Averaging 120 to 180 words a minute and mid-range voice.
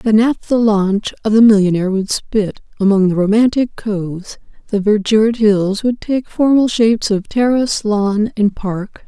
No: average, 160 wpm; high, 215 Hz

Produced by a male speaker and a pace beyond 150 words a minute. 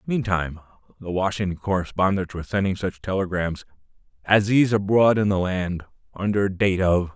No: male; average, 145 wpm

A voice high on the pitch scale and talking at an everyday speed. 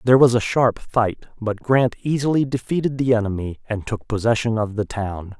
No: low, 115 Hz; average, 190 wpm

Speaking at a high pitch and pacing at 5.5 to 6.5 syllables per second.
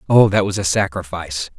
No: very low, 90 Hz; 5.9 syllables/s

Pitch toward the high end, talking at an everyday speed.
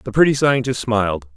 No: low, 120 Hz; average, 175 wpm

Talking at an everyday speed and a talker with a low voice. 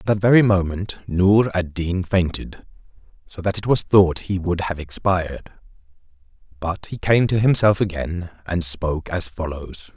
Yes: average, 155 wpm; very low, 90 Hz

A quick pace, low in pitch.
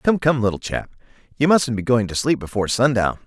Yes: fast, 220 wpm; low, 125 Hz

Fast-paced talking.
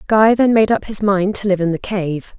Yes: fast, 275 wpm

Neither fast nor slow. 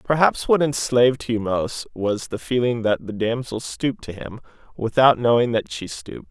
Yes: average, 180 wpm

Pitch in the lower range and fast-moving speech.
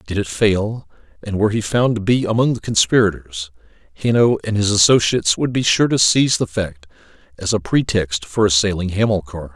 No: low, 105 Hz; average, 180 wpm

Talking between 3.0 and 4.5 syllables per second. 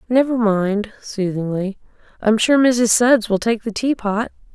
Yes: 4.1 syllables/s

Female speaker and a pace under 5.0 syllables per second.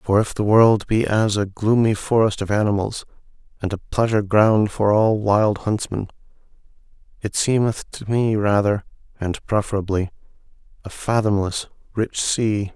No: male; 4.6 syllables/s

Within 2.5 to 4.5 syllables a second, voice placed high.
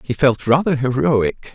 No: 4.1 syllables/s; low, 135 Hz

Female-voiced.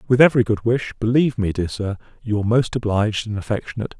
No: male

